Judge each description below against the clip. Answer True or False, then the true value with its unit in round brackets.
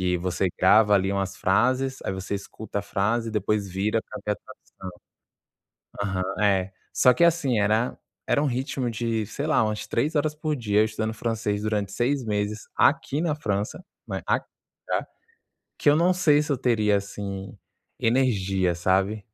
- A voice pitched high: False (110 Hz)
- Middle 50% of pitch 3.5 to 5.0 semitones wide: True (4.5 semitones)